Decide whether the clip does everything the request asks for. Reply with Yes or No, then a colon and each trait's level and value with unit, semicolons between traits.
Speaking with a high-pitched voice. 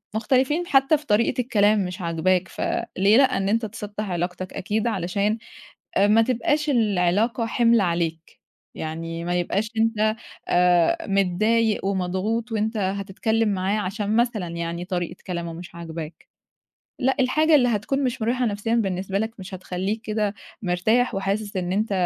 Yes: high, 205 Hz